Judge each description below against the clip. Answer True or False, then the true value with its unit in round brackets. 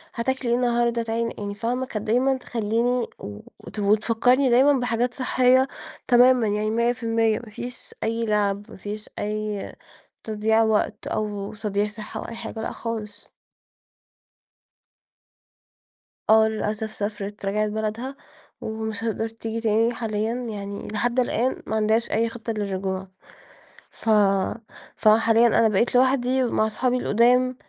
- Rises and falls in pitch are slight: True (2.3 semitones)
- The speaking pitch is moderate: False (225 Hz)